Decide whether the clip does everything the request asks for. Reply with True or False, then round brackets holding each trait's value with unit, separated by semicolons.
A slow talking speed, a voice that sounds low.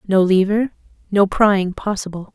False (130 wpm; 195 Hz)